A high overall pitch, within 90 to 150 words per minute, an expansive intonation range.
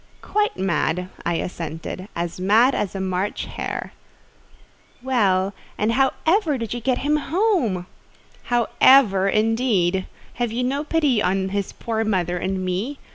Yes: high, 210 Hz; average, 145 wpm; wide, 5.7 semitones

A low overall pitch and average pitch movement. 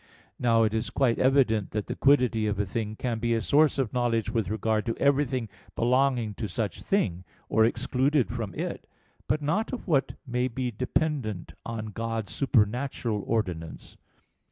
Yes: low, 115 Hz; average, 3.4 semitones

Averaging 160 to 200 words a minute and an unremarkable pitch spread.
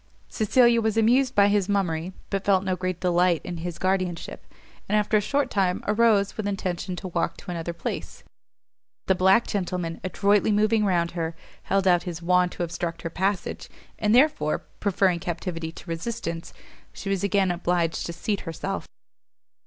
Yes: average, 170 wpm; average, 3.0 semitones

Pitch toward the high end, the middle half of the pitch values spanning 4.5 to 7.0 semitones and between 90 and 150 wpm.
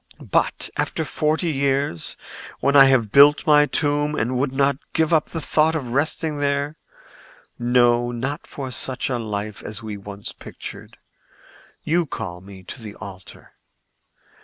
No: low, 135 Hz; average, 4.8 semitones; average, 140 wpm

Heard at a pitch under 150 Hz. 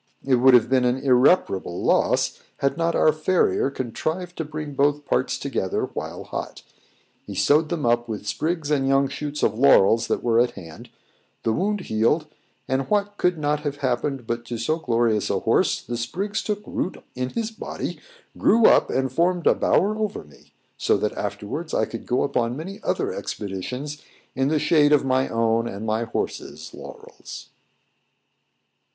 Yes: low, 135 Hz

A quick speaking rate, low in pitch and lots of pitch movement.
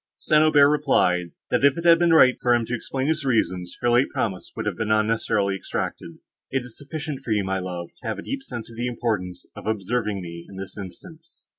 Yes: fast, 230 wpm; low, 115 Hz; wide, 6.6 semitones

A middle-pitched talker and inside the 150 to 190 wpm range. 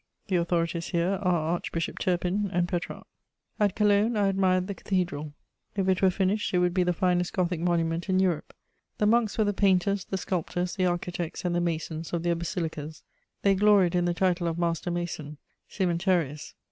Yes: medium, 180 Hz; average, 185 wpm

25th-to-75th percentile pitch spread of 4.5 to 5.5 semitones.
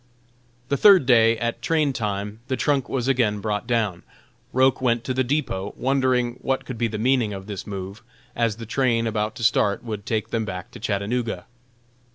No: average, 3.6 semitones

